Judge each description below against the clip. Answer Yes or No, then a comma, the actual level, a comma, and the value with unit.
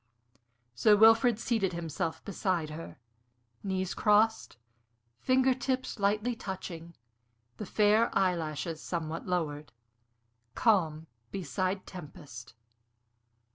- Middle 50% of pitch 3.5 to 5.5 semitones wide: Yes, average, 4.8 semitones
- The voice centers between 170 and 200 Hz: Yes, medium, 185 Hz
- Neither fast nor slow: No, slow, 90 wpm